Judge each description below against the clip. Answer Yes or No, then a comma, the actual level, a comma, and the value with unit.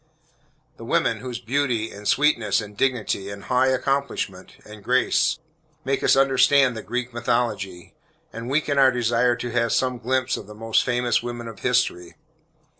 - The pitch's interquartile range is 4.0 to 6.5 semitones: No, average, 3.0 semitones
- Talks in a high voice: No, low, 120 Hz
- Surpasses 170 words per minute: No, average, 160 wpm